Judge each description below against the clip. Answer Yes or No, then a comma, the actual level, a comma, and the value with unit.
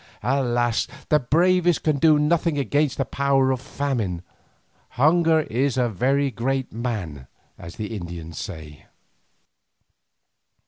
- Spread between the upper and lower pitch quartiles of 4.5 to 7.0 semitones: Yes, average, 5.1 semitones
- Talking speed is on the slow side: Yes, slow, 120 wpm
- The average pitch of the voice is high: No, low, 130 Hz